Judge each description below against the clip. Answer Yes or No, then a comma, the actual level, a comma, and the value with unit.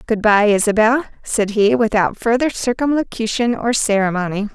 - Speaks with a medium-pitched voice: No, high, 220 Hz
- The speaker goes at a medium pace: No, slow, 130 wpm